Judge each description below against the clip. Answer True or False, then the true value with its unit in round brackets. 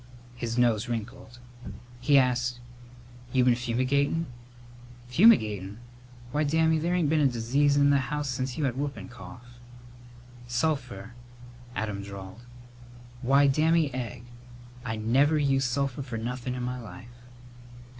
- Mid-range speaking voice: False (125 Hz)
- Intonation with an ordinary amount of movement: True (3.0 semitones)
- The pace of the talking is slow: True (130 wpm)